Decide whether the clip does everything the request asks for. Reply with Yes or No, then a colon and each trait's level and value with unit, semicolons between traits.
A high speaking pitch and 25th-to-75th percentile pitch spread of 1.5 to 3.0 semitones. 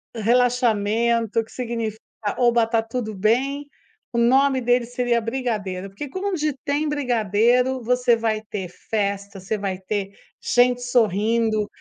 Yes: high, 230 Hz; average, 2.7 semitones